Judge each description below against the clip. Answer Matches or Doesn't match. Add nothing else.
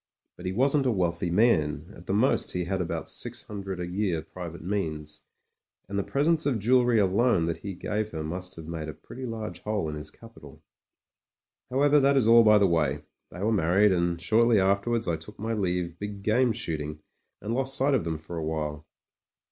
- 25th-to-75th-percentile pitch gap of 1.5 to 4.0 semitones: Doesn't match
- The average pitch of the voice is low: Matches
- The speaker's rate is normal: Doesn't match